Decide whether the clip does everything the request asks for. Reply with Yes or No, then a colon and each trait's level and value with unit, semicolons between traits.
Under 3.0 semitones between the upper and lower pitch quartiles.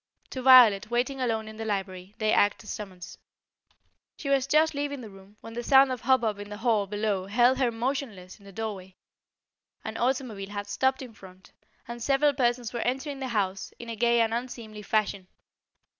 No: average, 3.9 semitones